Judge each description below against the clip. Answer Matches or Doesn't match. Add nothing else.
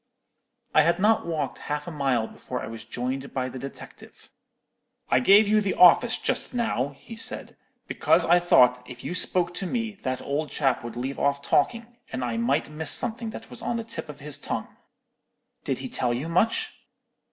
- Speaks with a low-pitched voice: Doesn't match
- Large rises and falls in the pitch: Matches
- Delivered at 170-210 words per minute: Matches